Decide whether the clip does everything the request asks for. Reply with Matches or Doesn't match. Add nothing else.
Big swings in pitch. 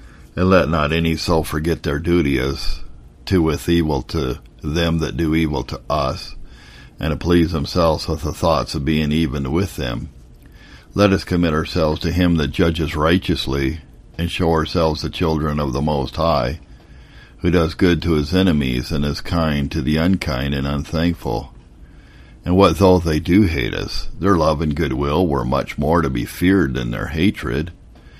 Doesn't match